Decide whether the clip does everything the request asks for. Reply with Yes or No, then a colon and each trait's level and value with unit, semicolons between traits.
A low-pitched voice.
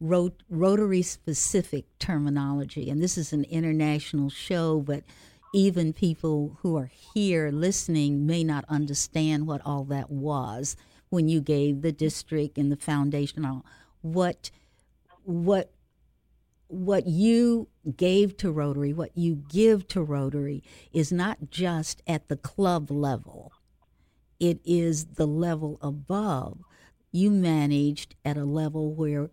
No: medium, 155 Hz